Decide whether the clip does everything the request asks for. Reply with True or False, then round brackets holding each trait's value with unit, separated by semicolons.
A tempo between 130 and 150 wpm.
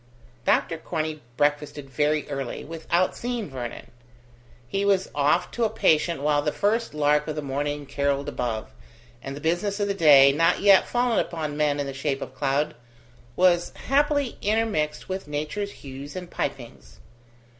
False (160 wpm)